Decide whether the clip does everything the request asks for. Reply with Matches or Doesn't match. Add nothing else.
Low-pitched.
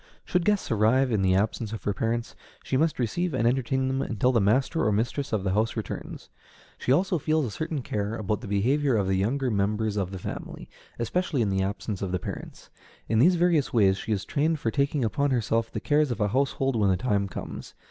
Matches